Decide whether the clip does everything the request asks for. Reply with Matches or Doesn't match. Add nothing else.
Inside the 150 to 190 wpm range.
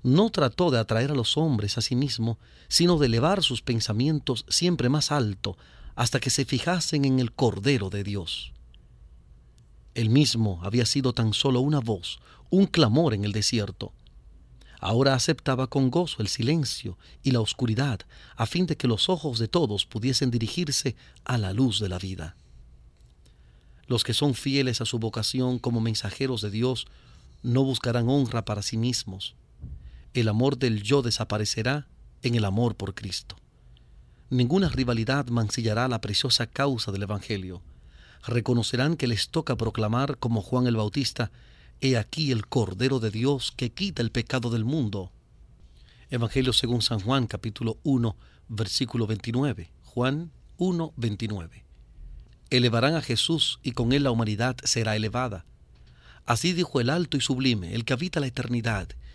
Matches